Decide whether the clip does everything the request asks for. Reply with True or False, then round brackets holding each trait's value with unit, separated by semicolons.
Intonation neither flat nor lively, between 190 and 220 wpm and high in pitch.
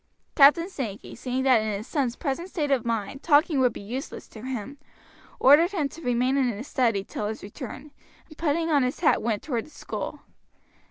True (4.3 semitones; 200 wpm; 265 Hz)